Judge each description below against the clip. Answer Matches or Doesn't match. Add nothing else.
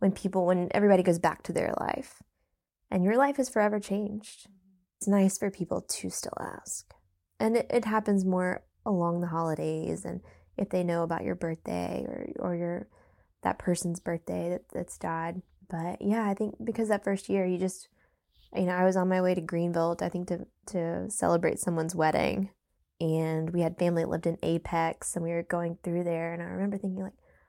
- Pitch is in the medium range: Matches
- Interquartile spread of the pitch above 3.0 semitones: Doesn't match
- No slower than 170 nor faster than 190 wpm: Doesn't match